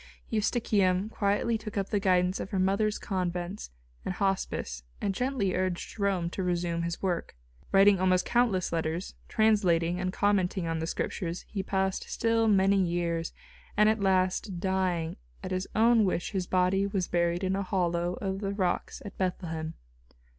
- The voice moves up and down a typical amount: No, narrow, 2.3 semitones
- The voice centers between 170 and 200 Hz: Yes, medium, 185 Hz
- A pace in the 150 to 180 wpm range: Yes, average, 160 wpm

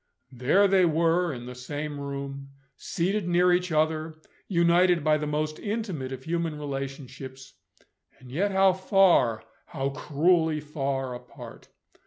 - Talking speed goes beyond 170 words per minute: No, slow, 135 wpm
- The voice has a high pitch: No, medium, 155 Hz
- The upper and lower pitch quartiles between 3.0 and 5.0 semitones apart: Yes, average, 4.4 semitones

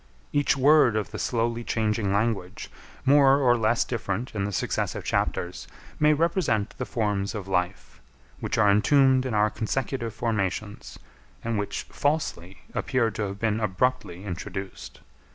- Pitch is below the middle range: Yes, low, 110 Hz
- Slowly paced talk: No, average, 145 wpm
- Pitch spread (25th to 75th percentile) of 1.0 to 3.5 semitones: No, average, 4.2 semitones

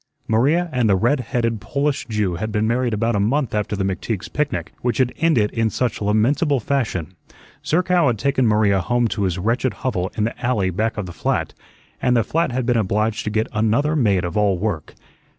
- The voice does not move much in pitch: No, average, 3.6 semitones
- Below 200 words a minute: No, fast, 205 wpm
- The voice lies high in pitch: No, low, 115 Hz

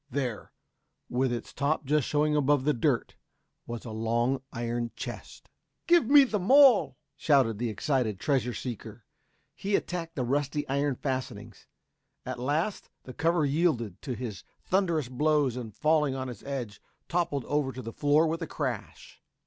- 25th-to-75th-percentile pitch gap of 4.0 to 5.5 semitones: Yes, average, 4.3 semitones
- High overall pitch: No, medium, 140 Hz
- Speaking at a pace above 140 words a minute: Yes, average, 155 wpm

